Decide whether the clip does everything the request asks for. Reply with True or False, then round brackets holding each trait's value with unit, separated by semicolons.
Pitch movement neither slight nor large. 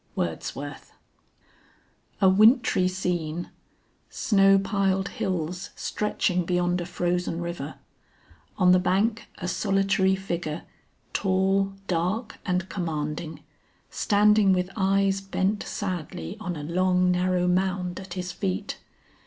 False (1.8 semitones)